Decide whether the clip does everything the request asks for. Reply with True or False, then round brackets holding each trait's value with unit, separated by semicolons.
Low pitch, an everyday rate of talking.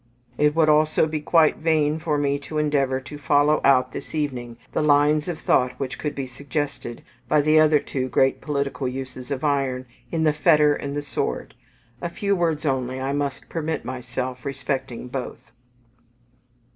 False (145 Hz; 170 wpm)